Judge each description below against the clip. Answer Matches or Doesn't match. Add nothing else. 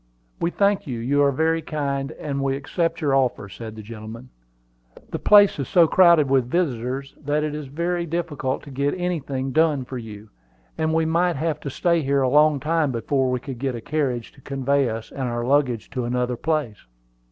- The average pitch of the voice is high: Doesn't match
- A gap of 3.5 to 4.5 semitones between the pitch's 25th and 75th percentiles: Matches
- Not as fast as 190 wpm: Doesn't match